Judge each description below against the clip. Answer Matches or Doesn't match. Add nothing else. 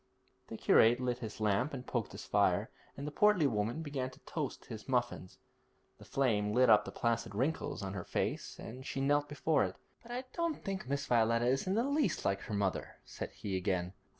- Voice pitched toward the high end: Doesn't match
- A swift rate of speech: Matches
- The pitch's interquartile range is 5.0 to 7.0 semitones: Matches